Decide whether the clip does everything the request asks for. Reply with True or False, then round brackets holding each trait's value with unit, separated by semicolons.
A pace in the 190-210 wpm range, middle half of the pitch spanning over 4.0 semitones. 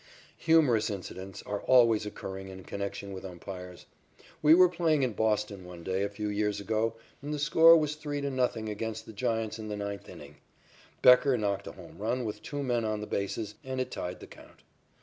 True (200 wpm; 4.4 semitones)